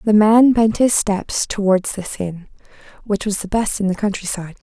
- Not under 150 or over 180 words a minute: No, fast, 205 wpm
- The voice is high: Yes, high, 205 Hz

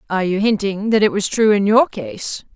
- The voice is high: Yes, high, 210 Hz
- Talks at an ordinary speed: No, fast, 235 wpm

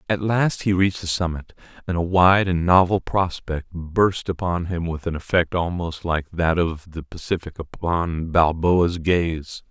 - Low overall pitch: Yes, very low, 85 Hz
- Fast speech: No, average, 165 wpm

